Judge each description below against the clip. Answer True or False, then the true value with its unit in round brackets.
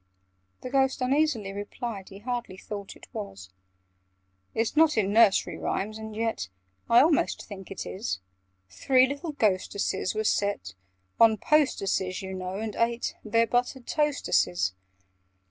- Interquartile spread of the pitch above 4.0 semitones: True (4.6 semitones)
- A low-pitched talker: False (220 Hz)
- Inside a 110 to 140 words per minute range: True (135 wpm)